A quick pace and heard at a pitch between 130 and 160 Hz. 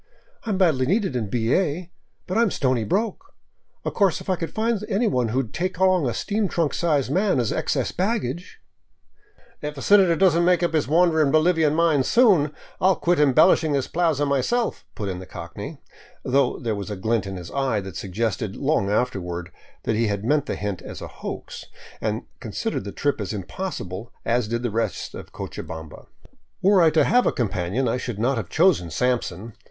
Yes: fast, 210 wpm; medium, 140 Hz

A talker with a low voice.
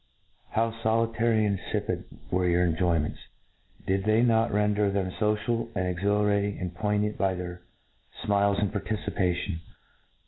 Yes: low, 100 Hz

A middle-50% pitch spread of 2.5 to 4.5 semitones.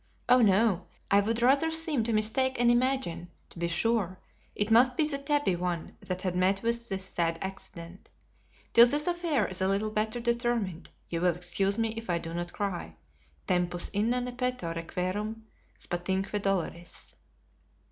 No: average, 5.1 semitones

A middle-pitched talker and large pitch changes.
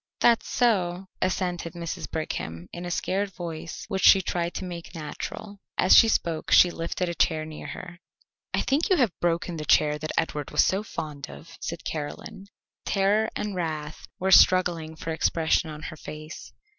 No: medium, 170 Hz; average, 3.3 semitones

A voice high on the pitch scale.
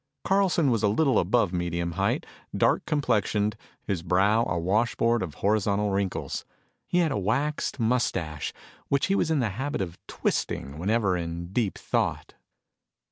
No: low, 105 Hz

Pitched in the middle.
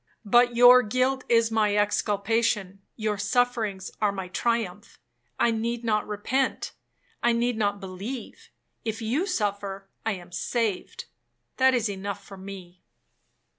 No: high, 215 Hz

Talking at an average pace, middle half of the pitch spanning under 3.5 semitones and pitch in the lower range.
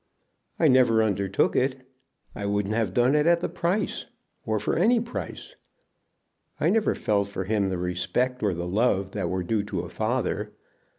No: average, 175 wpm; average, 5.0 semitones; low, 110 Hz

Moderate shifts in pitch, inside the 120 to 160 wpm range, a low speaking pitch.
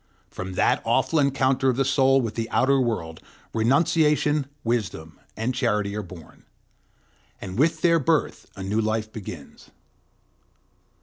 Yes: average, 4.9 semitones; slow, 135 wpm; low, 120 Hz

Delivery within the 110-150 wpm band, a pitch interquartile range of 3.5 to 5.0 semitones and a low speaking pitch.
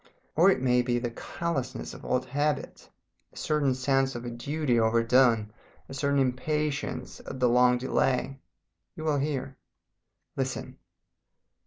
No: average, 140 wpm; average, 2.7 semitones; low, 130 Hz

